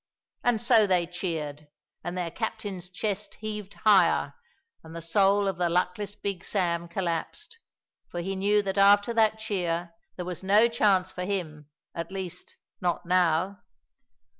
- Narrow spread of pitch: No, average, 3.0 semitones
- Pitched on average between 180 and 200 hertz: Yes, high, 190 Hz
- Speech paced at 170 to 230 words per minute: No, average, 150 wpm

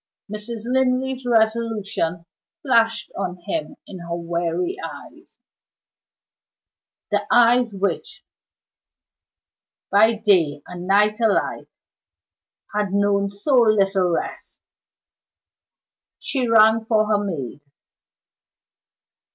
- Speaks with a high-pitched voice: Yes, high, 210 Hz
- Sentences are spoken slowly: Yes, slow, 85 wpm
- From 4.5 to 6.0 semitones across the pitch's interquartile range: No, average, 3.5 semitones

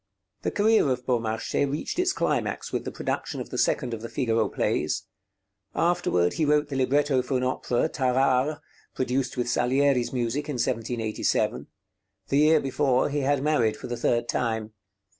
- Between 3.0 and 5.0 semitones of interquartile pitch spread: Yes, average, 3.4 semitones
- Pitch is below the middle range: Yes, low, 130 Hz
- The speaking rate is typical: Yes, average, 165 wpm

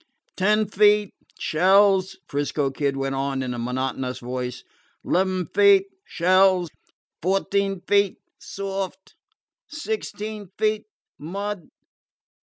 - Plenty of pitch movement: Yes, wide, 6.5 semitones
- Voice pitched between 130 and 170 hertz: No, high, 190 Hz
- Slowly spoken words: Yes, slow, 95 wpm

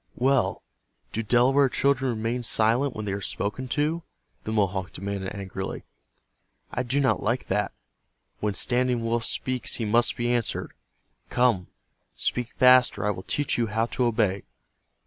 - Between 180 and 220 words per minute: No, average, 155 wpm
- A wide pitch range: No, average, 3.5 semitones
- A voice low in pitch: Yes, low, 115 Hz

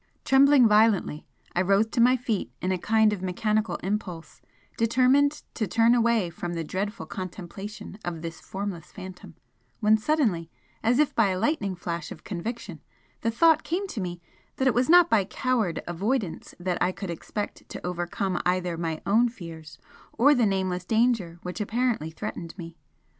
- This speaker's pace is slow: No, average, 170 wpm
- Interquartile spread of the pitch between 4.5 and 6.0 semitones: Yes, average, 4.9 semitones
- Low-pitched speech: No, high, 200 Hz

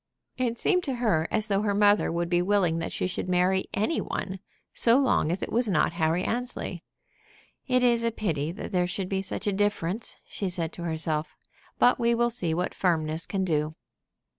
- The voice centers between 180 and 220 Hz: Yes, high, 190 Hz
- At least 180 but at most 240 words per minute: Yes, average, 200 wpm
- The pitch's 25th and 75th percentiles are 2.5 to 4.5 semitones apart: No, average, 5.1 semitones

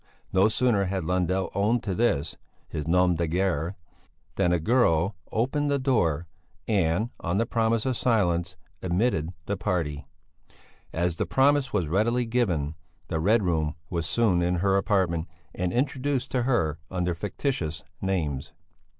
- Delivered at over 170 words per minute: No, average, 150 wpm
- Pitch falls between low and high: No, very low, 95 Hz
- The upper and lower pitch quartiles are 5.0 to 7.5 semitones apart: Yes, wide, 5.4 semitones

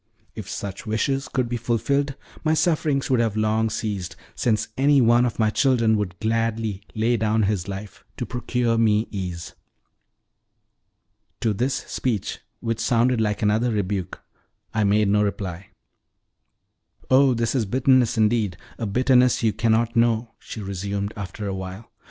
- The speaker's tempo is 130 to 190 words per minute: Yes, average, 150 wpm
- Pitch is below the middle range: Yes, low, 110 Hz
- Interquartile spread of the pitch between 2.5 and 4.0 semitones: Yes, average, 2.8 semitones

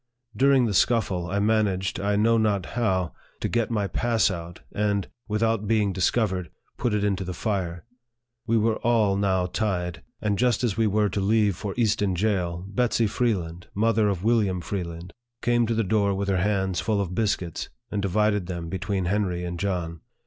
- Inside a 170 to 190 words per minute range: Yes, average, 180 wpm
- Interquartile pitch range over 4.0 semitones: No, average, 3.2 semitones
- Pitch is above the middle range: No, low, 100 Hz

